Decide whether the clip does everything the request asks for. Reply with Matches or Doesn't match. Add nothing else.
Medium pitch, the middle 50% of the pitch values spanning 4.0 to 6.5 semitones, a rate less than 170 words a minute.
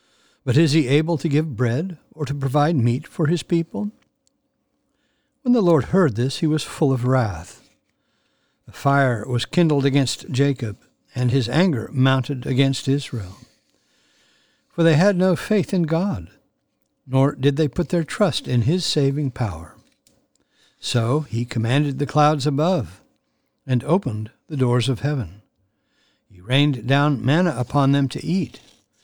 Matches